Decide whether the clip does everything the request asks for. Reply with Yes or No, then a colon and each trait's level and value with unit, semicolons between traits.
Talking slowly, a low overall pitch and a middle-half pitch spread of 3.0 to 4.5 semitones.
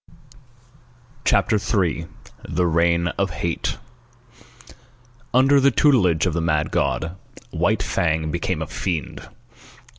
Yes: slow, 110 wpm; very low, 85 Hz; average, 4.1 semitones